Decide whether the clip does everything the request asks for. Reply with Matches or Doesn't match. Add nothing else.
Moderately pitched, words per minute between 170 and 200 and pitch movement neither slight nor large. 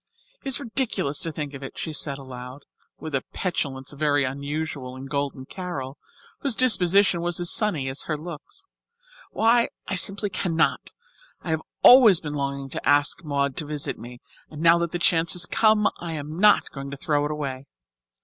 Matches